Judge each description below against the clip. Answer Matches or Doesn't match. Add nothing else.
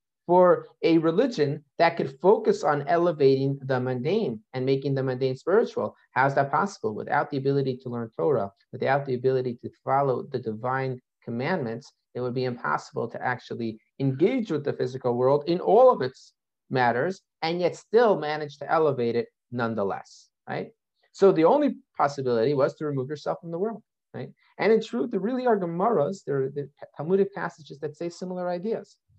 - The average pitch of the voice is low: Doesn't match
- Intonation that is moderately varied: Doesn't match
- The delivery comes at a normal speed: Matches